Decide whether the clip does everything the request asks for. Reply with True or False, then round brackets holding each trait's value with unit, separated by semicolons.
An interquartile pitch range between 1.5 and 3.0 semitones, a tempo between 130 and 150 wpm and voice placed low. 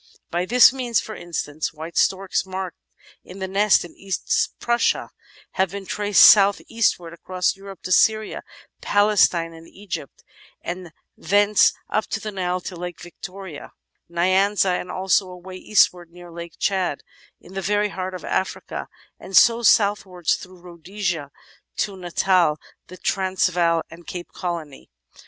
False (2.5 semitones; 145 wpm; 185 Hz)